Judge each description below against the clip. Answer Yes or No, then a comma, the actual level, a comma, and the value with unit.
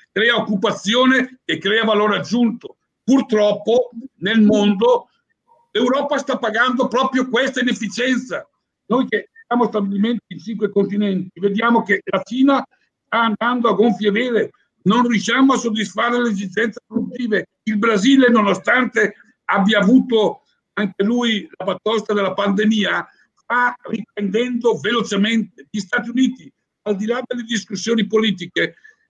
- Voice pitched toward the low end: No, high, 225 Hz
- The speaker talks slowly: No, average, 125 wpm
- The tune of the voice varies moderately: Yes, average, 3.0 semitones